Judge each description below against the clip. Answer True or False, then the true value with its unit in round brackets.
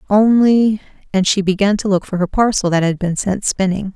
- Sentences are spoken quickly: True (210 wpm)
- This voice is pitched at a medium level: False (195 Hz)